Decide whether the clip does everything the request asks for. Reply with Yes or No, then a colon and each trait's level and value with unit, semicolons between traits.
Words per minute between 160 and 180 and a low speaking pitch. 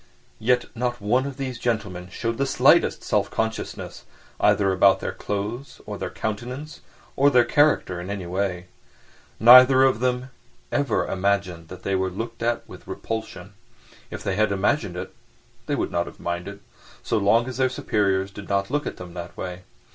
Yes: average, 170 wpm; low, 105 Hz